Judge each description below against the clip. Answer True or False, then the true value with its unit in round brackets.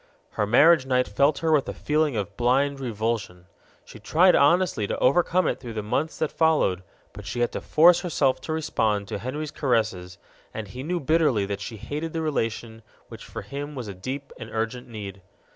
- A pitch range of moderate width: False (6.1 semitones)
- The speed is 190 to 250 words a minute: True (195 wpm)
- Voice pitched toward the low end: True (125 Hz)